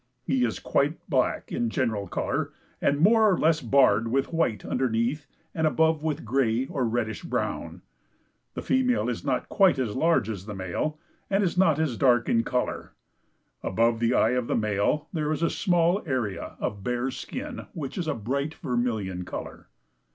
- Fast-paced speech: No, average, 175 wpm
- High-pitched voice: No, low, 130 Hz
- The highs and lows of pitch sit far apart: Yes, wide, 5.7 semitones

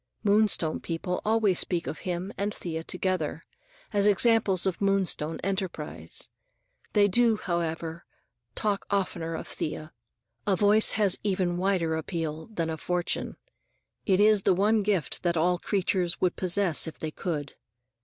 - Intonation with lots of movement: No, average, 3.5 semitones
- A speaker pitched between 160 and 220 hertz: Yes, medium, 185 Hz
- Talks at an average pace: Yes, average, 145 wpm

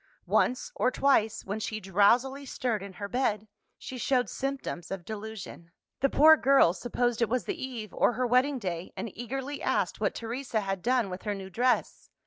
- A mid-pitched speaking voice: No, high, 235 Hz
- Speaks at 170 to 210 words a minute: Yes, average, 185 wpm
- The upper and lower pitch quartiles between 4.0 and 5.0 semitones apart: Yes, average, 4.3 semitones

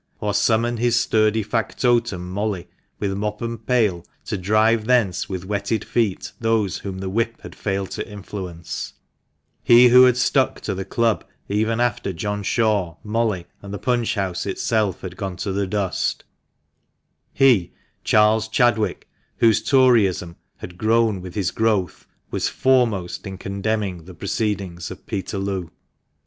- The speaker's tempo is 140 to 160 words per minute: Yes, average, 155 wpm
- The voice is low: Yes, low, 105 Hz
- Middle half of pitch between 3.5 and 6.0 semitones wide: No, average, 3.0 semitones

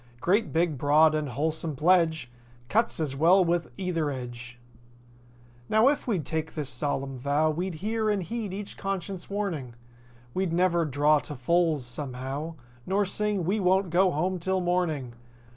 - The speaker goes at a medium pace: Yes, average, 155 wpm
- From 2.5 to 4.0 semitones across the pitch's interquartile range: No, average, 4.5 semitones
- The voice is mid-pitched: Yes, medium, 165 Hz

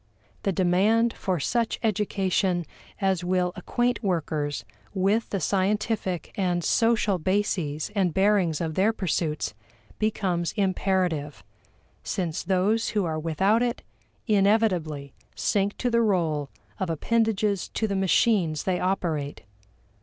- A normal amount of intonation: Yes, average, 3.7 semitones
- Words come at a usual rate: No, slow, 120 wpm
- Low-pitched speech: No, high, 190 Hz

